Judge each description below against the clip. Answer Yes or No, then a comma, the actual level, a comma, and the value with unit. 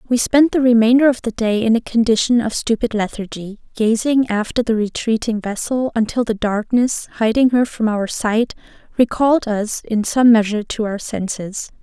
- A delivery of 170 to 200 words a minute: Yes, average, 175 wpm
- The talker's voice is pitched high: Yes, high, 230 Hz